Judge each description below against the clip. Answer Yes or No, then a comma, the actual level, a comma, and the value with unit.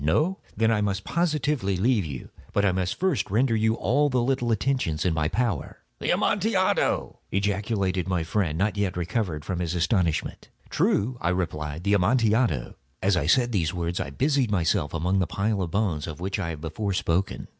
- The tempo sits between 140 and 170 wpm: No, average, 190 wpm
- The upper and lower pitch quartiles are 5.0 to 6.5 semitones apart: Yes, average, 5.3 semitones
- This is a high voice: No, low, 100 Hz